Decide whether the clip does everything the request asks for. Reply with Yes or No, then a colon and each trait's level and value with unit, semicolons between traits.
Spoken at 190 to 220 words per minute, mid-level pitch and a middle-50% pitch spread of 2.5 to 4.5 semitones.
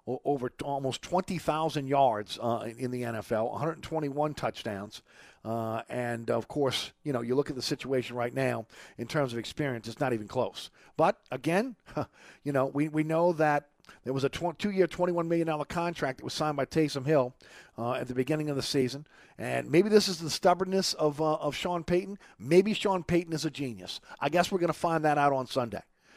No: fast, 205 wpm; medium, 145 Hz; average, 5.0 semitones